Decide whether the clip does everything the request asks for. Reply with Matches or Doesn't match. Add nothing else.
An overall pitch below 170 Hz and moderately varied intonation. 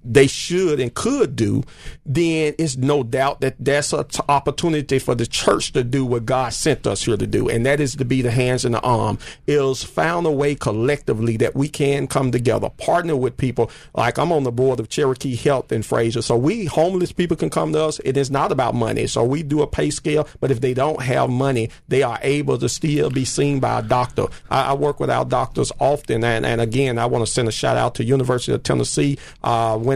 Matches